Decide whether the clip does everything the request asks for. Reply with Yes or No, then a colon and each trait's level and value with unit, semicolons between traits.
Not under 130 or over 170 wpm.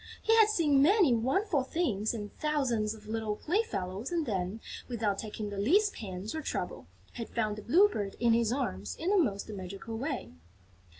No: average, 180 wpm